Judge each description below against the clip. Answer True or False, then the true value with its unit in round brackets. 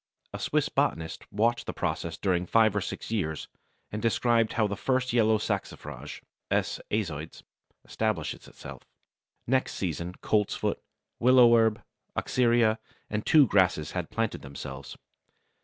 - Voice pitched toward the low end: True (110 Hz)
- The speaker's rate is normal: False (130 wpm)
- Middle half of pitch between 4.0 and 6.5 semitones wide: True (4.7 semitones)